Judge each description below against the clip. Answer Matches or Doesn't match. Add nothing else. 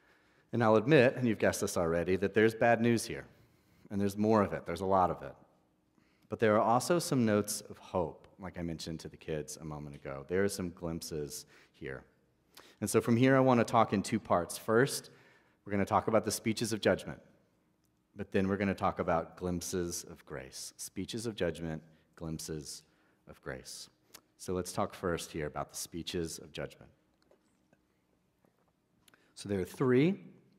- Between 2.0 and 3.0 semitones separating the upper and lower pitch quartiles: Doesn't match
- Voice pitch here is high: Doesn't match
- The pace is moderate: Matches